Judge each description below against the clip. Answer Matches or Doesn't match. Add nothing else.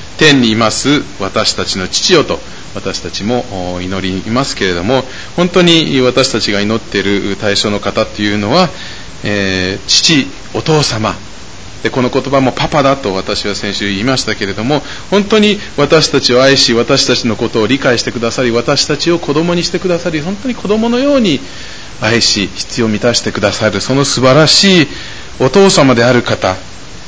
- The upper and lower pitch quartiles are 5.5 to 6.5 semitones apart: Matches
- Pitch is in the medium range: Doesn't match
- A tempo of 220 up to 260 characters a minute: Doesn't match